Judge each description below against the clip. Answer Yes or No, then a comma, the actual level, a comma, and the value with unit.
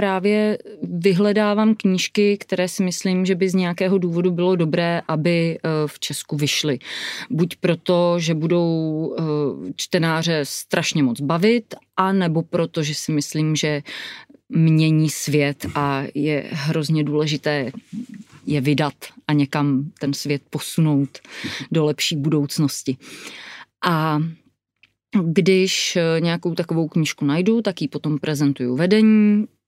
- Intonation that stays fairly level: No, average, 3.6 semitones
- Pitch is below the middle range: No, medium, 160 Hz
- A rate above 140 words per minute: No, average, 120 wpm